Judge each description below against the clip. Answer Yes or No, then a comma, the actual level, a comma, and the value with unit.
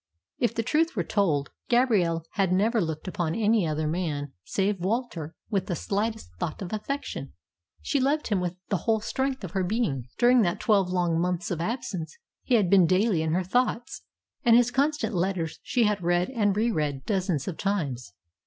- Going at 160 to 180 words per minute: No, average, 190 wpm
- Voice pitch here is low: No, high, 190 Hz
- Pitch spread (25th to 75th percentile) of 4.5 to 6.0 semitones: Yes, average, 5.2 semitones